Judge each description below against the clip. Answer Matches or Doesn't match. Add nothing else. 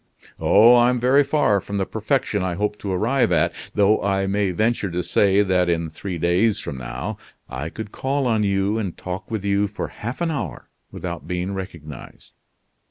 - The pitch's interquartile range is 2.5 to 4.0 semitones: Matches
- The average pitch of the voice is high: Doesn't match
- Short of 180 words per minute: Doesn't match